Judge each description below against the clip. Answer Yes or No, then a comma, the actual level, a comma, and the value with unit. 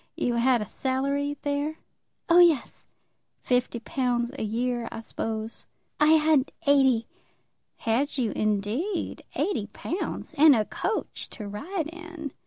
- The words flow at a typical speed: No, slow, 130 wpm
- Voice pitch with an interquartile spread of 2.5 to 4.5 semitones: No, average, 5.1 semitones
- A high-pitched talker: Yes, very high, 265 Hz